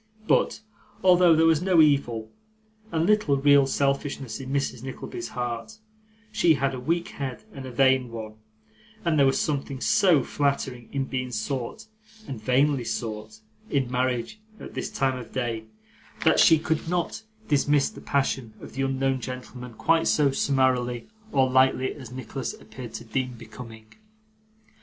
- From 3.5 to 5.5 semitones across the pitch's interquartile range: No, average, 2.8 semitones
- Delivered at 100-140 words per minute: No, average, 155 wpm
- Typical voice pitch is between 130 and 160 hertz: Yes, low, 135 Hz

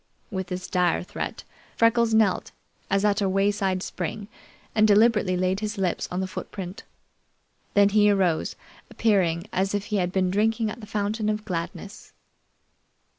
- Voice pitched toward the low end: No, high, 200 Hz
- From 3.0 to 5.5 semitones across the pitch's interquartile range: No, narrow, 2.4 semitones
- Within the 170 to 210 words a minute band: No, average, 155 wpm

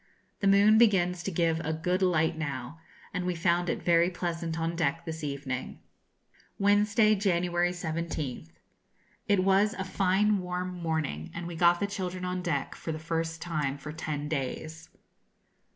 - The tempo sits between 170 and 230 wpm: No, average, 160 wpm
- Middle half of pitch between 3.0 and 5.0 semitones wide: No, narrow, 2.4 semitones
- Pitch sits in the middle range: Yes, medium, 170 Hz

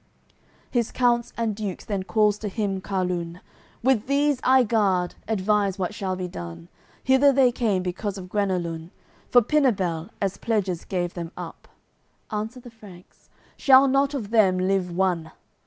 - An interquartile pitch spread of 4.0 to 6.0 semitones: Yes, average, 4.5 semitones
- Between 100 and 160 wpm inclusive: Yes, average, 155 wpm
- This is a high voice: Yes, high, 200 Hz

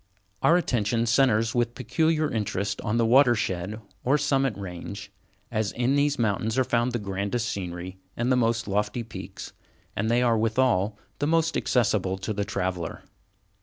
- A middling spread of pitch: Yes, average, 3.8 semitones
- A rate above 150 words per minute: Yes, average, 160 wpm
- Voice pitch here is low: Yes, low, 115 Hz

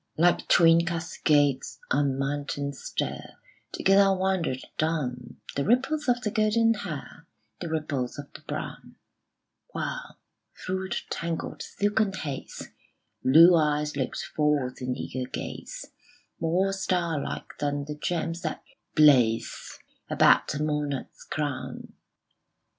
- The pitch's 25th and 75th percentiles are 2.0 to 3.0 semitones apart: No, average, 4.7 semitones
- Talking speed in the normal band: No, slow, 115 wpm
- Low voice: No, medium, 155 Hz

